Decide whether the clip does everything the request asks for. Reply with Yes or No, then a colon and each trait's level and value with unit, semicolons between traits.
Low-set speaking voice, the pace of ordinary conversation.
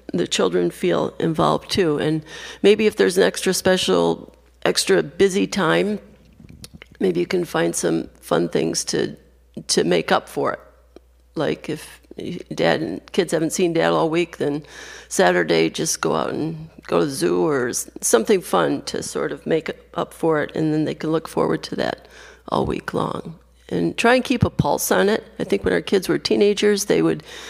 No: medium, 160 Hz; average, 190 wpm